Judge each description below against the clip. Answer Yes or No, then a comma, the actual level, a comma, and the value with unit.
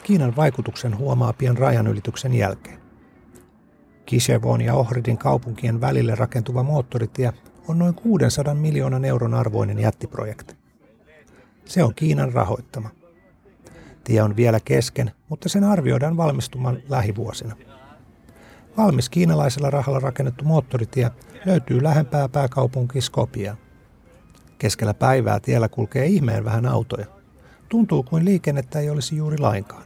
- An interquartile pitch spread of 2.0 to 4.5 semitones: Yes, average, 4.0 semitones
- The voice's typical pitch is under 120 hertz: No, low, 125 Hz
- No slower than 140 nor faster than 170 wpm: No, average, 115 wpm